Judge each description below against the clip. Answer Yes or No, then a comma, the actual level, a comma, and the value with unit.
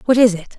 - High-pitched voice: Yes, high, 220 Hz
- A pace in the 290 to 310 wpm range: Yes, fast, 305 wpm